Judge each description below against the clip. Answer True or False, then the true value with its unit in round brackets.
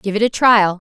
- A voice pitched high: True (210 Hz)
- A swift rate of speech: True (265 wpm)